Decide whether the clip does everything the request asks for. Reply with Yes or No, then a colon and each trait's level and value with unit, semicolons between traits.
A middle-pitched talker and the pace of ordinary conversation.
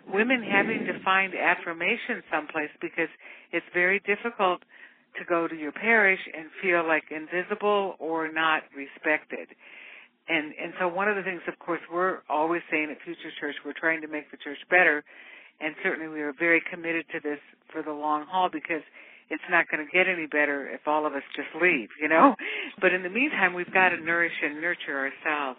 Yes: medium, 165 Hz; average, 195 wpm